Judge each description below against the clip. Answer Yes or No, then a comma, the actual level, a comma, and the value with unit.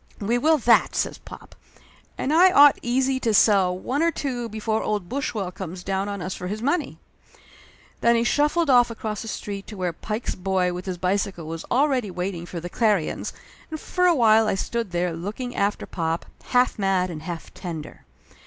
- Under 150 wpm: No, average, 200 wpm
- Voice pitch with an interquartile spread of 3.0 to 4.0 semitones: No, average, 5.2 semitones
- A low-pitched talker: No, high, 210 Hz